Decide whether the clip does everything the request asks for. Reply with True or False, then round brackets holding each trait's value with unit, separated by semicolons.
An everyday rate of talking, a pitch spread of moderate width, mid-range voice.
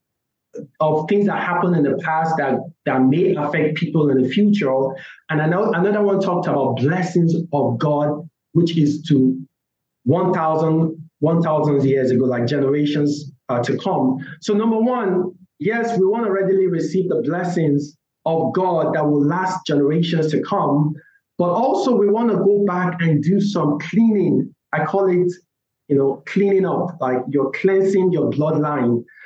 True (160 wpm; 4.5 semitones; 160 Hz)